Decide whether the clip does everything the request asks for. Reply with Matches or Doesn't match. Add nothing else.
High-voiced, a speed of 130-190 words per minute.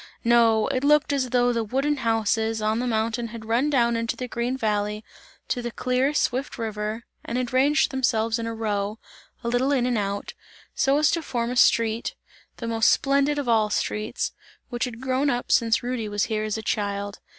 Doesn't match